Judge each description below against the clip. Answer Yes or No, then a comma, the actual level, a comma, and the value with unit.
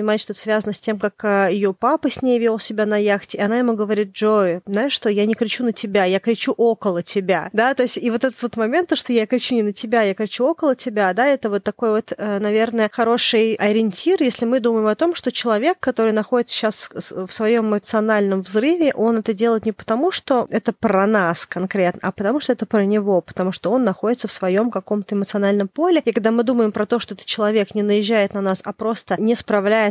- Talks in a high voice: Yes, high, 220 Hz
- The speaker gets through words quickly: Yes, fast, 225 wpm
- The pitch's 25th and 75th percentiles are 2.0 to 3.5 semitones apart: Yes, narrow, 2.4 semitones